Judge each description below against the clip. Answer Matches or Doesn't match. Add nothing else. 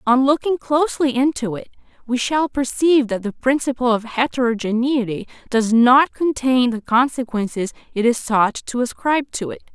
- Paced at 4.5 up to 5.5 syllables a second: Matches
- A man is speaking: Doesn't match